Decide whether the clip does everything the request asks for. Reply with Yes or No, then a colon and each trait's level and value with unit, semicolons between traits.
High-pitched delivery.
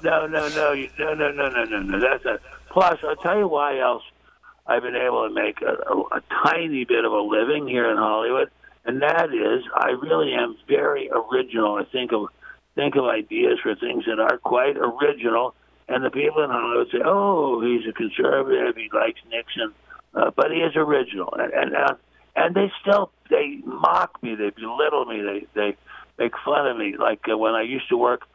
Yes: high, 195 Hz